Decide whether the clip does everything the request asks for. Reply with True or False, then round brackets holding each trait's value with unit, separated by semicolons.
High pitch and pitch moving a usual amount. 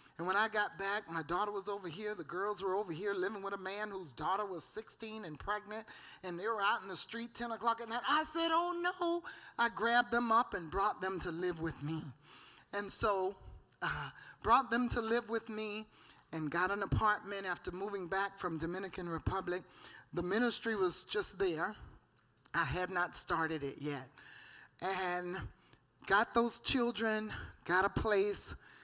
True (200 Hz; 4.3 semitones)